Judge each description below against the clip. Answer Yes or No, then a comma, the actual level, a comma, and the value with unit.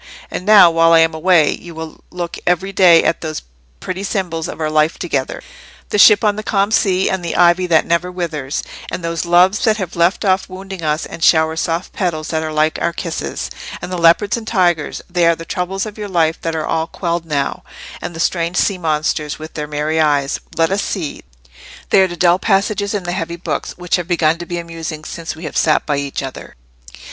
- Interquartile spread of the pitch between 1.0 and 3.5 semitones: Yes, narrow, 2.6 semitones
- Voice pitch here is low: No, medium, 170 Hz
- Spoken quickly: Yes, fast, 215 wpm